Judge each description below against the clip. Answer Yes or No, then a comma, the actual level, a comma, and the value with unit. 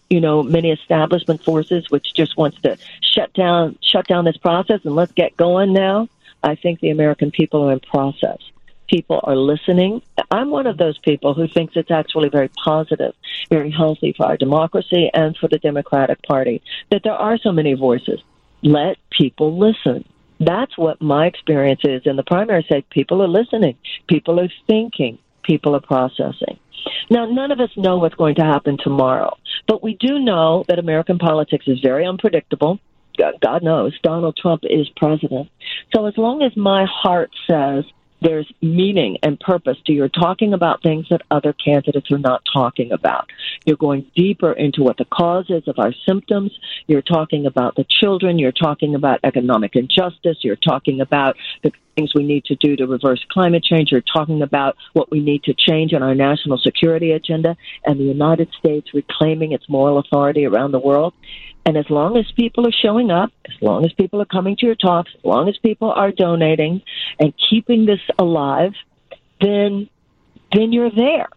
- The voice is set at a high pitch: No, medium, 160 Hz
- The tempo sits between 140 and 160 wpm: No, average, 185 wpm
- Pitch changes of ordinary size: Yes, average, 4.3 semitones